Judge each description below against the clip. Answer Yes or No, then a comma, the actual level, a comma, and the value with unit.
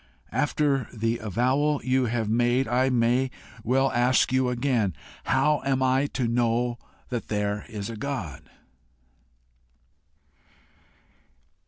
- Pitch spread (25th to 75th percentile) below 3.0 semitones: Yes, narrow, 2.5 semitones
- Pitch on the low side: Yes, low, 125 Hz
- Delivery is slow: Yes, slow, 115 wpm